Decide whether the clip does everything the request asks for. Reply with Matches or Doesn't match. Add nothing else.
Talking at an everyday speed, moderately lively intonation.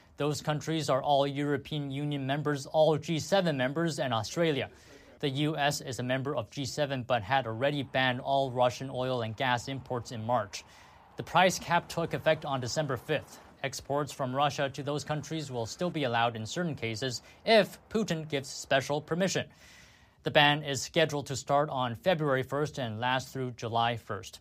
Matches